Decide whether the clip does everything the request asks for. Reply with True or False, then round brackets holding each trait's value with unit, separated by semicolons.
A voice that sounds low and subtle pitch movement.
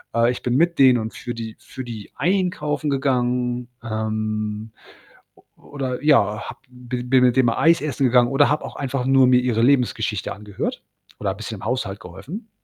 False (125 Hz; 3.7 semitones)